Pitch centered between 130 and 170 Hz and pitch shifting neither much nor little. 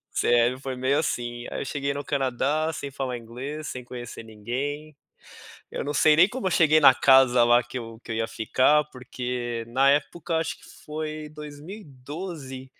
Yes: low, 135 Hz; average, 3.7 semitones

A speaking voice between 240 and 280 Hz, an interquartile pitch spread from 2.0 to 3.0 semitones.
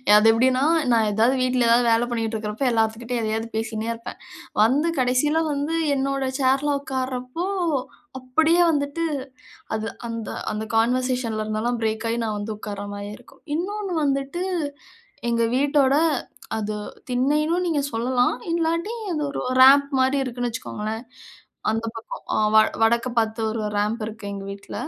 No: high, 245 Hz; average, 3.8 semitones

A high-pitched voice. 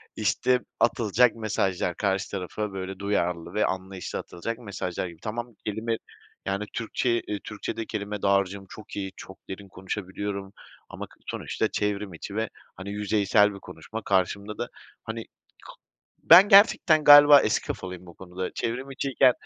No: low, 100 Hz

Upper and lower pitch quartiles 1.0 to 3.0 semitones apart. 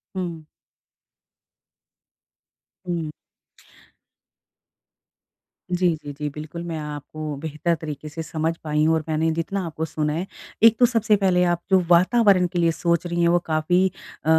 Yes: narrow, 2.5 semitones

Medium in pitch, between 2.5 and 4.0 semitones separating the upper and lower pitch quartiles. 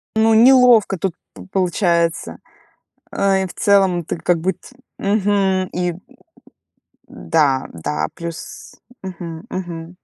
Yes: medium, 180 Hz; average, 2.8 semitones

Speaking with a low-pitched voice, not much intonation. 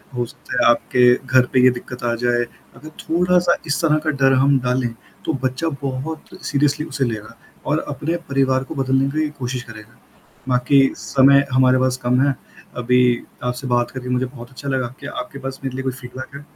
Yes: low, 130 Hz; narrow, 2.0 semitones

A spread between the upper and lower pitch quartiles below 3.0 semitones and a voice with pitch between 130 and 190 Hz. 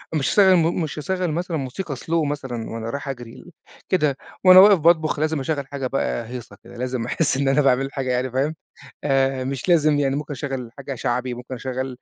No: average, 3.4 semitones; low, 135 Hz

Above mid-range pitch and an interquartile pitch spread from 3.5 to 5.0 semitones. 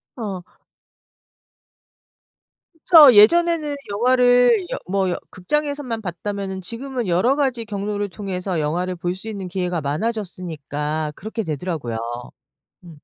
No: high, 200 Hz; wide, 5.5 semitones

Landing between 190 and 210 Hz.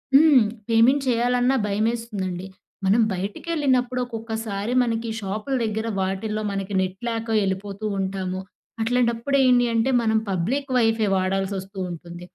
No: high, 220 Hz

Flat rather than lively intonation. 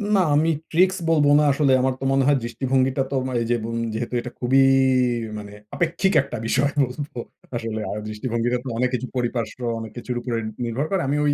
No: average, 3.4 semitones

